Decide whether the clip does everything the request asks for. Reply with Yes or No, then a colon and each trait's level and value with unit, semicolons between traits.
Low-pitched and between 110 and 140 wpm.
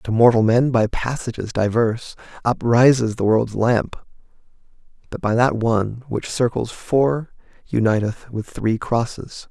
Yes: low, 115 Hz; slow, 135 wpm